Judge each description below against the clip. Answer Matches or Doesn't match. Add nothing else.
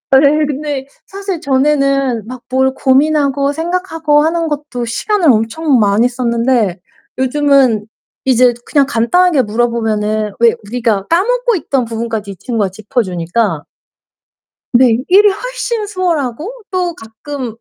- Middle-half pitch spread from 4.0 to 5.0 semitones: Doesn't match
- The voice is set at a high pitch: Matches